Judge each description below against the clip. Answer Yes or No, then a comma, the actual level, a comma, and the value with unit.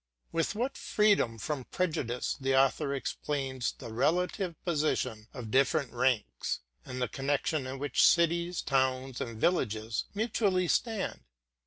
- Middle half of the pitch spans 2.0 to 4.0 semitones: No, wide, 5.4 semitones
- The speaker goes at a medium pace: No, slow, 130 wpm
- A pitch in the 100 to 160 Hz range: Yes, low, 135 Hz